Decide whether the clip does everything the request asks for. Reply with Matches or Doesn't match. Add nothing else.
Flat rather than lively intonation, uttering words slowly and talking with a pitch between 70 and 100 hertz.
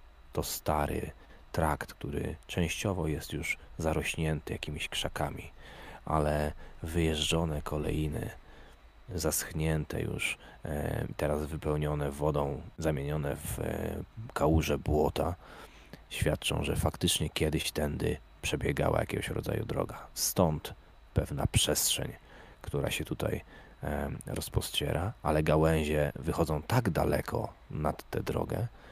Matches